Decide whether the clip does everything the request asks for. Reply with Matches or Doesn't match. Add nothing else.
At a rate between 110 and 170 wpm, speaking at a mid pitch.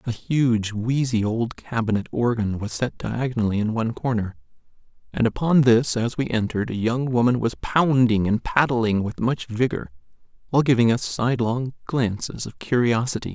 Doesn't match